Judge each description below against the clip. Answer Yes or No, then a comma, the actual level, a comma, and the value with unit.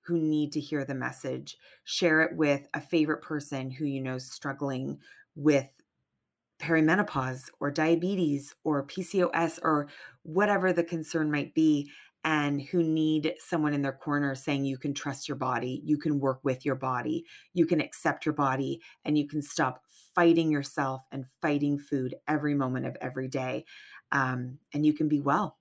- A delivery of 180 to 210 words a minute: No, average, 170 wpm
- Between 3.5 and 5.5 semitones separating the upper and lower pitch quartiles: No, narrow, 2.6 semitones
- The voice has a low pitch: No, medium, 150 Hz